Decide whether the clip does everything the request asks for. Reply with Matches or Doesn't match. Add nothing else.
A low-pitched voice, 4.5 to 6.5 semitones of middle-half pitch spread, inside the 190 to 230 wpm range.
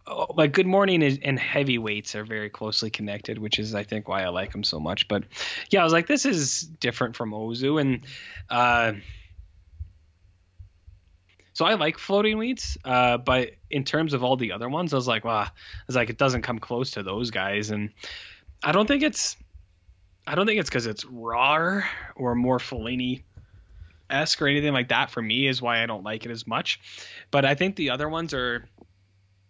Matches